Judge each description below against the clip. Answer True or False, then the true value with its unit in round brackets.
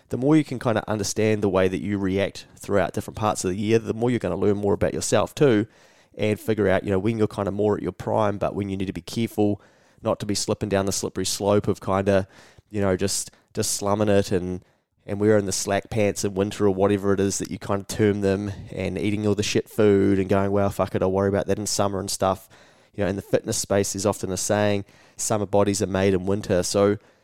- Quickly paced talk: True (260 wpm)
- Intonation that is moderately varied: False (1.4 semitones)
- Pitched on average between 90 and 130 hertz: True (100 Hz)